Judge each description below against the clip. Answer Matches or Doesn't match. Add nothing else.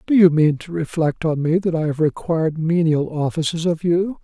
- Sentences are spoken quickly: Matches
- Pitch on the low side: Doesn't match